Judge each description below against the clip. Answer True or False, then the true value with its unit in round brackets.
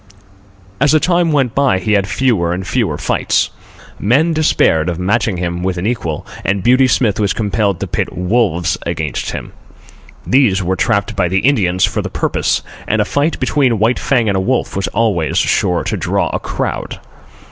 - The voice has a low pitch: True (105 Hz)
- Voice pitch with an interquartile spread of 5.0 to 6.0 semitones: True (5.6 semitones)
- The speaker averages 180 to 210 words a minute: True (185 wpm)